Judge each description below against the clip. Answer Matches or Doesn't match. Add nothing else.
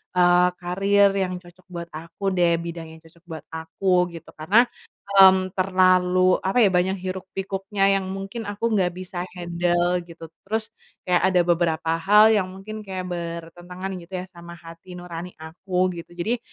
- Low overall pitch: Doesn't match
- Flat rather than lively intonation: Matches